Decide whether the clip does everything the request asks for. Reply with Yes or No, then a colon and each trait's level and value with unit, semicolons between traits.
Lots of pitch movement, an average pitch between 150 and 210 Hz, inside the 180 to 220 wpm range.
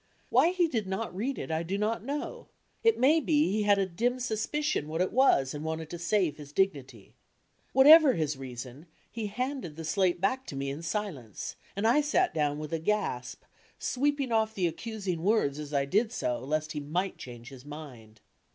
Yes: wide, 7.8 semitones; medium, 185 Hz; average, 195 wpm